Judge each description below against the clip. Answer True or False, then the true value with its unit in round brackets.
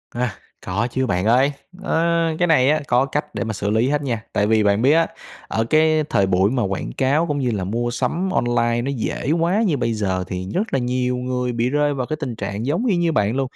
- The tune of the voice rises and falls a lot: False (5.0 semitones)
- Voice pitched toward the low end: True (125 Hz)